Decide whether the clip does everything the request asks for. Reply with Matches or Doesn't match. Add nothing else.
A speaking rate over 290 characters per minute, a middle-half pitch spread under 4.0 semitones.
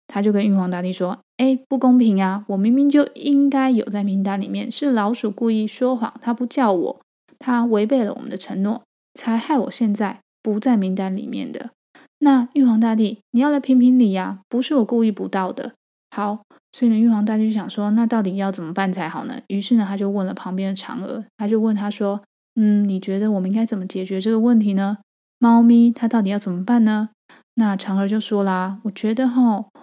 Matches